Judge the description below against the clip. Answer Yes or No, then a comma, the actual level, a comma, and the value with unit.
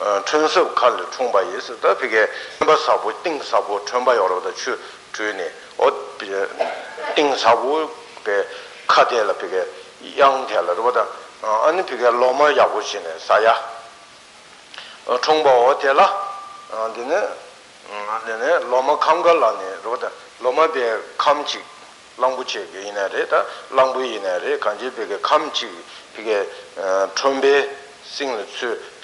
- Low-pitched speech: No, high, 195 Hz